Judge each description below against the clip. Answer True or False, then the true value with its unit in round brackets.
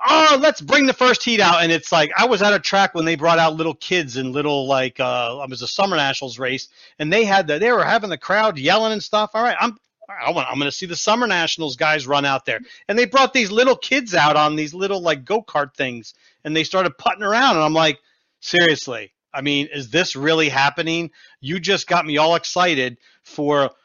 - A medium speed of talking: False (235 wpm)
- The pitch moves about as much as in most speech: False (5.7 semitones)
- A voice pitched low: False (165 Hz)